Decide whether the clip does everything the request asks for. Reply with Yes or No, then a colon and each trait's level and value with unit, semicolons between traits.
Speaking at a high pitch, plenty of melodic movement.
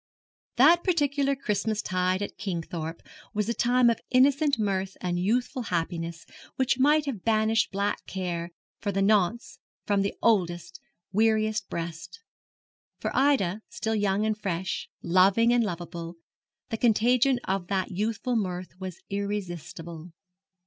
No: high, 205 Hz; average, 4.4 semitones